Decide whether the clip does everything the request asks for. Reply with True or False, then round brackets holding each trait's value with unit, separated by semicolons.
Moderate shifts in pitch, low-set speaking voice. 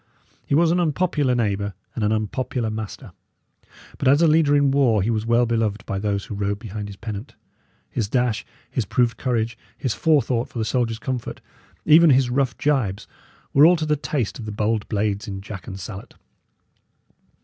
True (4.6 semitones; 115 Hz)